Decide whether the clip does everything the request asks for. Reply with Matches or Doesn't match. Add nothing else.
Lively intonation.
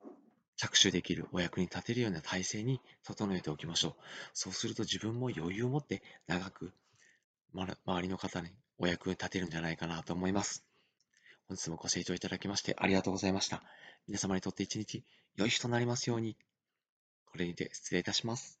Doesn't match